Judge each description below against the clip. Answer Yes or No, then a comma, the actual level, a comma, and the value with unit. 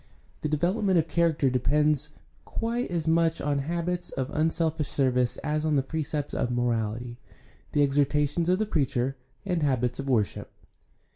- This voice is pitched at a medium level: Yes, medium, 150 Hz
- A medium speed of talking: Yes, average, 150 wpm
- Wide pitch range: No, average, 3.9 semitones